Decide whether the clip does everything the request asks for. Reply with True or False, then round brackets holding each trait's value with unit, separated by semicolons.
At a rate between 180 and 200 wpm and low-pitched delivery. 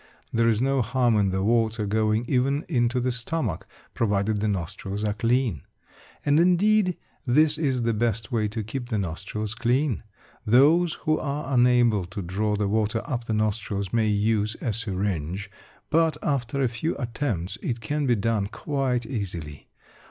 False (165 wpm; 115 Hz)